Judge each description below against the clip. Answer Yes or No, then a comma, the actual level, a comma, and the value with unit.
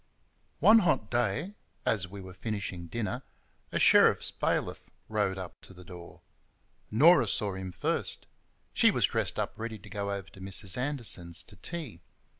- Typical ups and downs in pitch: Yes, average, 4.2 semitones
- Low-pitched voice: Yes, low, 100 Hz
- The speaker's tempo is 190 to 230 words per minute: No, average, 160 wpm